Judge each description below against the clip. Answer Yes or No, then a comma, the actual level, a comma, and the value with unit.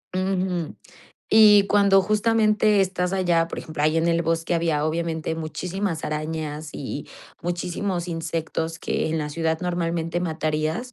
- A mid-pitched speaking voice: Yes, medium, 170 Hz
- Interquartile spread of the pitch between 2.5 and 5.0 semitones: Yes, average, 2.9 semitones